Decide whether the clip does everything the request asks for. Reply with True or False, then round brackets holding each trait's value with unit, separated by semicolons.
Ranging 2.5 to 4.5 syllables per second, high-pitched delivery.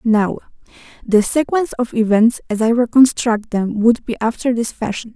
False (5.1 syllables/s; 230 Hz)